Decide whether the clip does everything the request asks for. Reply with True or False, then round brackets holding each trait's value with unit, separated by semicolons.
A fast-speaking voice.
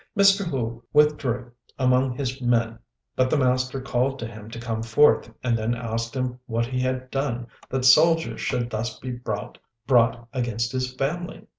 False (165 wpm)